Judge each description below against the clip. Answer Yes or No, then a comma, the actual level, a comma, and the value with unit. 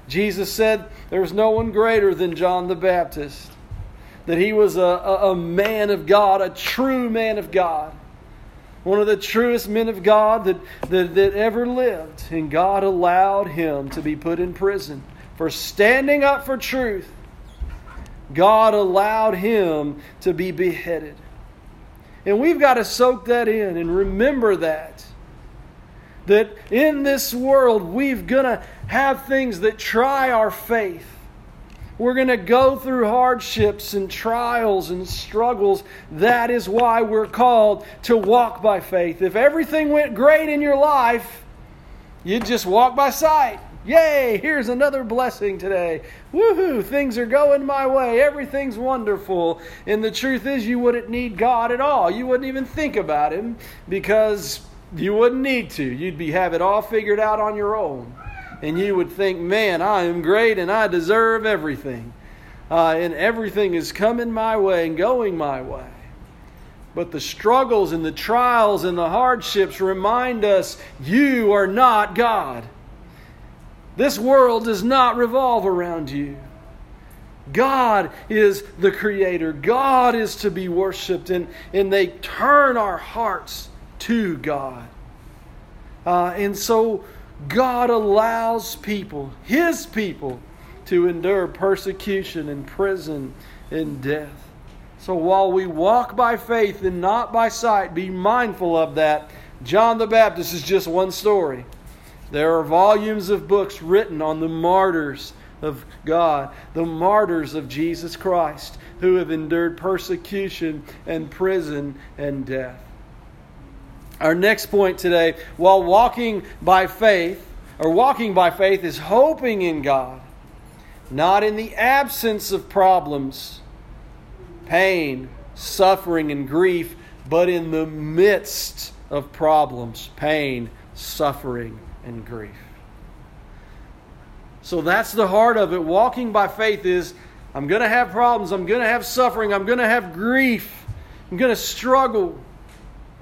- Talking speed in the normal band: Yes, average, 145 wpm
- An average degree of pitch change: No, wide, 5.8 semitones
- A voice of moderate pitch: No, high, 195 Hz